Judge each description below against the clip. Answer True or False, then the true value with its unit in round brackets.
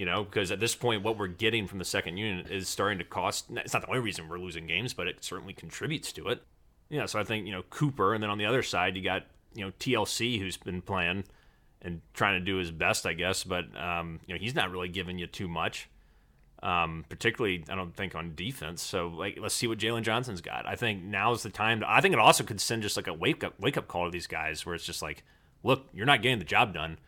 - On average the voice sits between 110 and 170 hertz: False (95 Hz)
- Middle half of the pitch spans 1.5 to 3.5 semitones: False (4.1 semitones)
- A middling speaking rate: False (270 wpm)